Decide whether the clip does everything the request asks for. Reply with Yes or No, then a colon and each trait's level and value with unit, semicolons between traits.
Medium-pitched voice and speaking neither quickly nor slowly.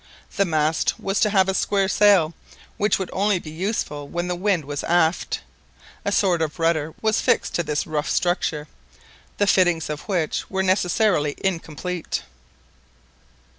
Yes: medium, 175 Hz; average, 155 wpm